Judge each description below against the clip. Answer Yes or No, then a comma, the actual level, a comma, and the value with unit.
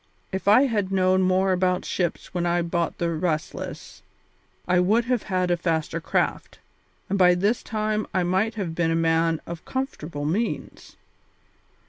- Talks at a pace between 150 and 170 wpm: Yes, average, 160 wpm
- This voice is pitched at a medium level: Yes, medium, 180 Hz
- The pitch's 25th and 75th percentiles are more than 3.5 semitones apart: No, average, 3.0 semitones